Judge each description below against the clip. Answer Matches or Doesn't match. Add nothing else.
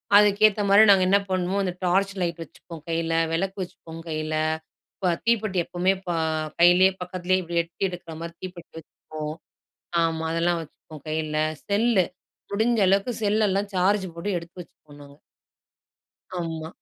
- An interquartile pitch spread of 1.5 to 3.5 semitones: Matches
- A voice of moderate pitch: Matches